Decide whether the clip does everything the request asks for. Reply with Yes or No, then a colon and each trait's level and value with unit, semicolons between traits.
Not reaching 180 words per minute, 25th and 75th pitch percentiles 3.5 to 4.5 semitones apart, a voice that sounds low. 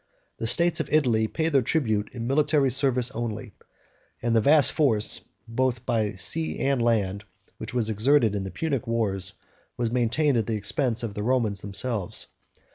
Yes: average, 170 wpm; average, 3.8 semitones; low, 115 Hz